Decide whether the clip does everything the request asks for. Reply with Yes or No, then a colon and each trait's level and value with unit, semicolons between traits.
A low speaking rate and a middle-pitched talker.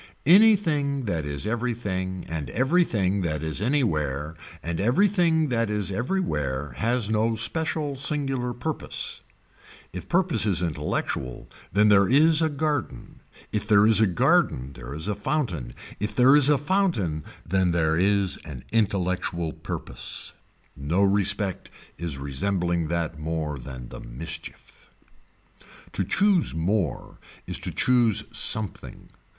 No: slow, 130 wpm; low, 100 Hz